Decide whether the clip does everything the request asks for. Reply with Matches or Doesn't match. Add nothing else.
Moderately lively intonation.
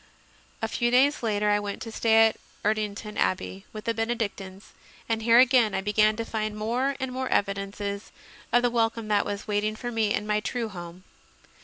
Doesn't match